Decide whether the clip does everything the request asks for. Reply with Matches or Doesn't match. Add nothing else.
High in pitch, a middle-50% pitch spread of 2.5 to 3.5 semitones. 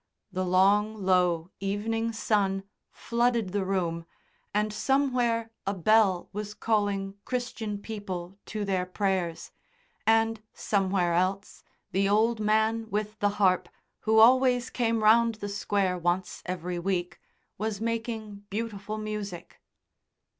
Matches